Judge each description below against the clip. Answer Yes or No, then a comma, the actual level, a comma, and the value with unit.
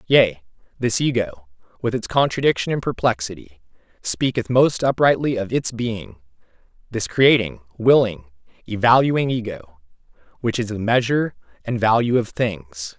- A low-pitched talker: Yes, low, 110 Hz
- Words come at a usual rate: No, slow, 120 wpm